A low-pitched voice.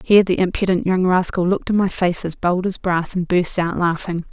No: medium, 180 Hz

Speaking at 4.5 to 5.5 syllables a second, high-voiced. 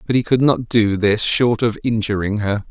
No: 4.8 syllables/s; low, 110 Hz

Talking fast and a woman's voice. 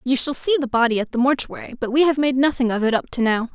Yes: fast, 305 wpm; female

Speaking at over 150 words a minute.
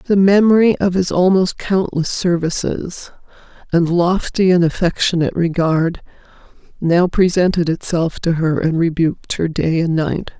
No: slow, 135 wpm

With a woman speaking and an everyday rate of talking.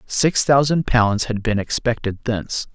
No: male; average, 155 wpm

